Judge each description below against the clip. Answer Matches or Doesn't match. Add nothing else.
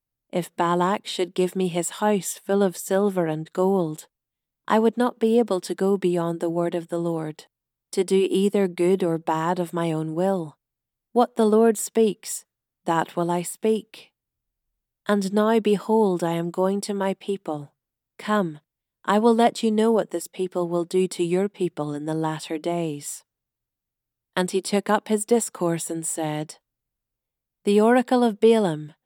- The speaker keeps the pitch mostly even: Doesn't match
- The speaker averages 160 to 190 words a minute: Matches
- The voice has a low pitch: Doesn't match